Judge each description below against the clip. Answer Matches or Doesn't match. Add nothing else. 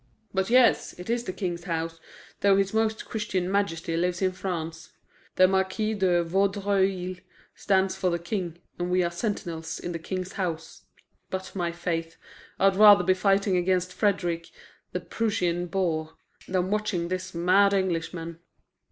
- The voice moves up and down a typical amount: Doesn't match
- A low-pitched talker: Doesn't match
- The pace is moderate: Matches